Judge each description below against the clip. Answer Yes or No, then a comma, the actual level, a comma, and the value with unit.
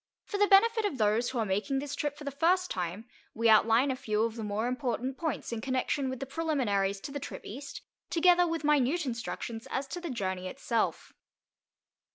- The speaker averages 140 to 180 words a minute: No, average, 200 wpm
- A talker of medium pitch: No, very high, 260 Hz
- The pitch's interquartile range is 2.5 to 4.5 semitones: No, average, 5.1 semitones